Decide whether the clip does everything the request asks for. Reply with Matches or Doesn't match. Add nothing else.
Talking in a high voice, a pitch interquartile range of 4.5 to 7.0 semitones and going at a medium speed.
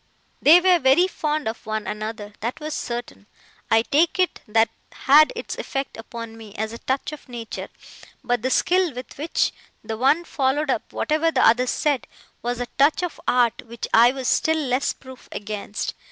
Matches